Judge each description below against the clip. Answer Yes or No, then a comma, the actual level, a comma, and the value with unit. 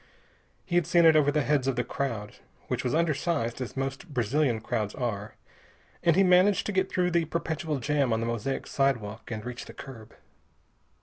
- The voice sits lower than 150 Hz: Yes, low, 135 Hz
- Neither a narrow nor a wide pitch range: No, wide, 5.7 semitones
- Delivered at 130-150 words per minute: No, average, 185 wpm